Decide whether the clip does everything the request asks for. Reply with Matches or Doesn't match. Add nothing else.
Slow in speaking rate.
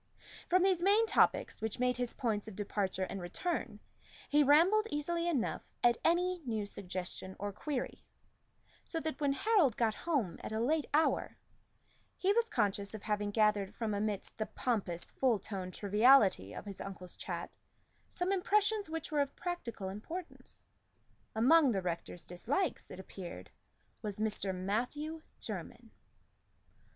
Doesn't match